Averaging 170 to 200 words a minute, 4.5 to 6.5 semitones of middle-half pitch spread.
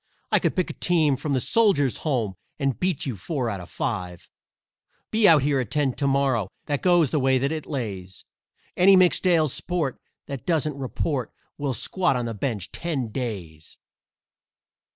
Yes: average, 175 wpm; average, 5.1 semitones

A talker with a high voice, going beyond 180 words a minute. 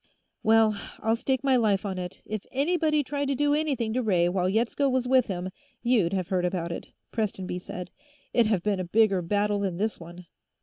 Yes: high, 215 Hz; fast, 205 wpm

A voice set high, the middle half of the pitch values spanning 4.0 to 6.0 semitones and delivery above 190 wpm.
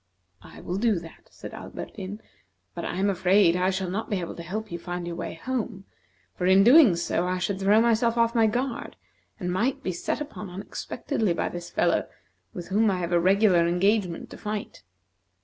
No: high, 195 Hz; average, 3.6 semitones; average, 200 wpm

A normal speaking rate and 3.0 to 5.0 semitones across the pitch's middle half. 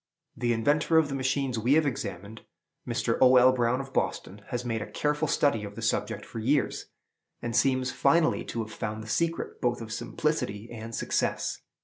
Yes: average, 190 wpm; average, 3.9 semitones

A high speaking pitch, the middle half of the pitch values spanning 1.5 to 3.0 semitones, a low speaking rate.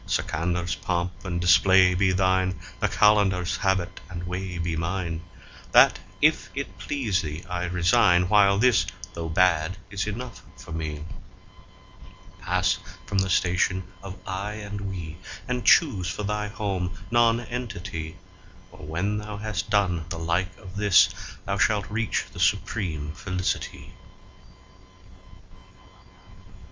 No: very low, 95 Hz; average, 2.7 semitones; slow, 120 wpm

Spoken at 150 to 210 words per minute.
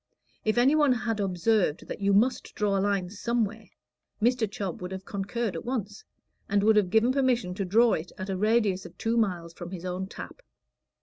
Yes: average, 200 wpm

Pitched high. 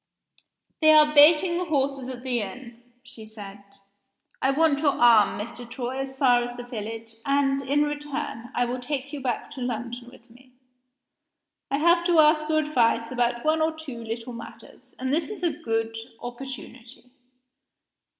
Yes: very high, 260 Hz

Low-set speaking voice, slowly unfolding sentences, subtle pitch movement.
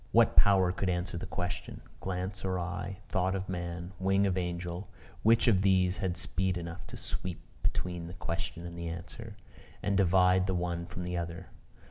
No: very low, 90 Hz; average, 180 wpm; narrow, 1.6 semitones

